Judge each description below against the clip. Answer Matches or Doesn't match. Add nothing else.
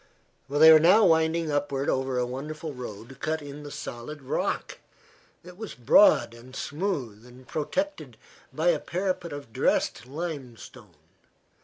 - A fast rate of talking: Doesn't match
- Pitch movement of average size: Matches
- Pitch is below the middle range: Doesn't match